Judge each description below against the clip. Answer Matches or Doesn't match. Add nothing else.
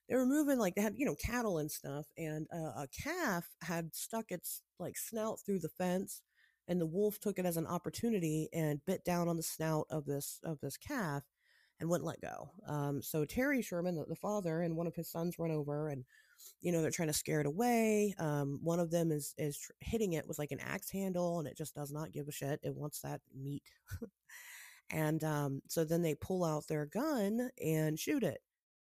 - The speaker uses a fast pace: Matches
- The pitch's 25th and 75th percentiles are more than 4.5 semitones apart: Doesn't match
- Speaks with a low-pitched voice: Doesn't match